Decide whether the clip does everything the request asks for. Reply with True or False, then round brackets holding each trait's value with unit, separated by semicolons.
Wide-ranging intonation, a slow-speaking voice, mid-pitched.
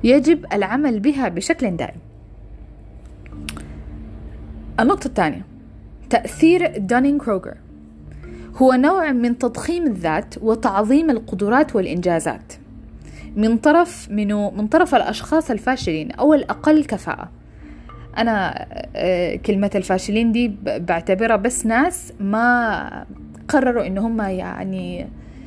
False (6.0 semitones; 90 wpm; 225 Hz)